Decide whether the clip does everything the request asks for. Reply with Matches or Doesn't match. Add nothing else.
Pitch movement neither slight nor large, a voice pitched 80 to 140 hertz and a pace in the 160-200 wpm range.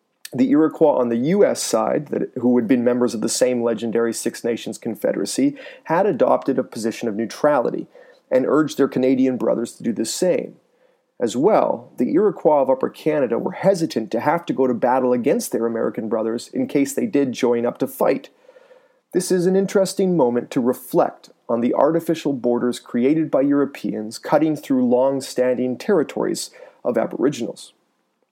Doesn't match